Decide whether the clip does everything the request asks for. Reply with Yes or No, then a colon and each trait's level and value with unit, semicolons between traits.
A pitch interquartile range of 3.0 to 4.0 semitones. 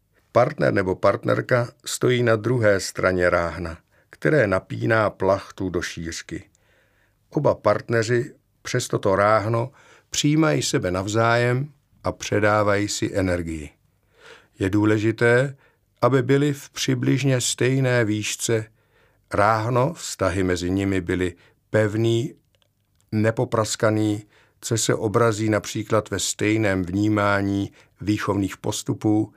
Yes: average, 3.3 semitones